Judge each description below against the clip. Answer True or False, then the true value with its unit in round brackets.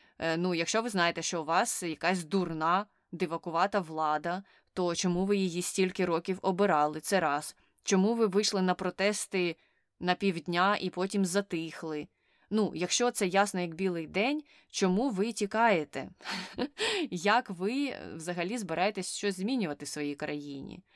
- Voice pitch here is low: False (185 Hz)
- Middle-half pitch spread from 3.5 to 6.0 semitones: False (3.1 semitones)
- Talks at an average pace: True (140 wpm)